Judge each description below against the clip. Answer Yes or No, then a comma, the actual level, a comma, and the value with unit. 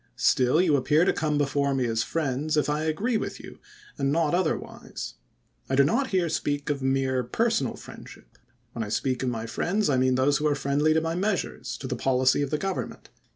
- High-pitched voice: No, medium, 145 Hz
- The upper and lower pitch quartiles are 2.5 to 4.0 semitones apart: Yes, average, 3.6 semitones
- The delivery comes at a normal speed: No, fast, 215 wpm